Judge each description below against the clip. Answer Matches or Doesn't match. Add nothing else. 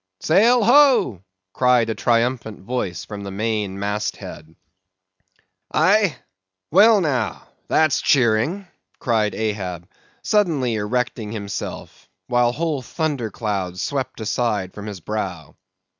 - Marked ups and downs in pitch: Matches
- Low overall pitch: Matches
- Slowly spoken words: Matches